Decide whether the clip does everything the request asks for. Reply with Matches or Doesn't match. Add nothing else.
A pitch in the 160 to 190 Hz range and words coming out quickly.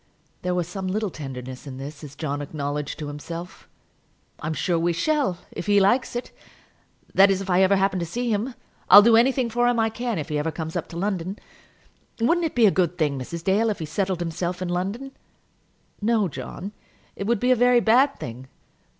Matches